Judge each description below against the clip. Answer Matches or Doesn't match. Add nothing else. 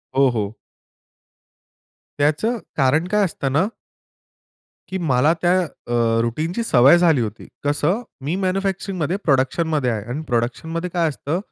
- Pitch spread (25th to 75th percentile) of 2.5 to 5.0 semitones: Doesn't match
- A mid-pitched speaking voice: Matches